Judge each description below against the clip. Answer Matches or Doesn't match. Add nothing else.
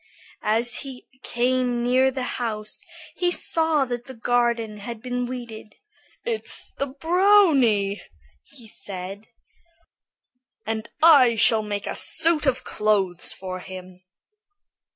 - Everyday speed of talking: Doesn't match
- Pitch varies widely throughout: Doesn't match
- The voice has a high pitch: Matches